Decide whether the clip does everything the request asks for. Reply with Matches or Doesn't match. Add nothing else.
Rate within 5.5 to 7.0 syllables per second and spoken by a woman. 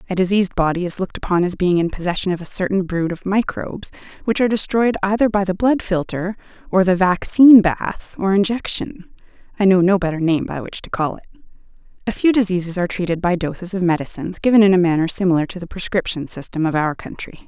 Matches